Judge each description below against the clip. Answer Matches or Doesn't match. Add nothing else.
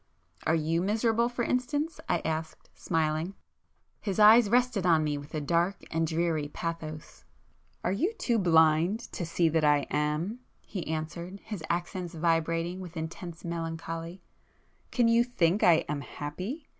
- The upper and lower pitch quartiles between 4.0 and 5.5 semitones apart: Matches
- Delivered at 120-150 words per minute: Matches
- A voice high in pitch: Doesn't match